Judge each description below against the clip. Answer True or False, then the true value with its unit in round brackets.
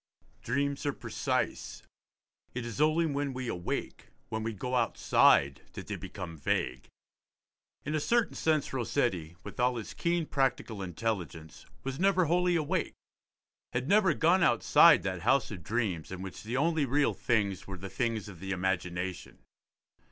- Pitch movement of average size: False (7.5 semitones)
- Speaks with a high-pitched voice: False (120 Hz)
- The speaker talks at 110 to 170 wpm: True (155 wpm)